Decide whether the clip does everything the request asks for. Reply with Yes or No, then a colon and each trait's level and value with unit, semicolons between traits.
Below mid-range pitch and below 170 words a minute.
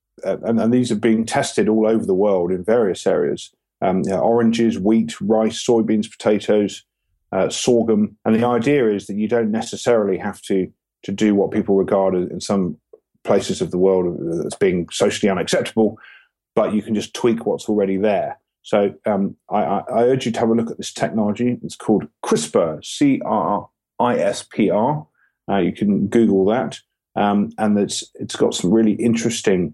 No: low, 110 Hz; average, 185 wpm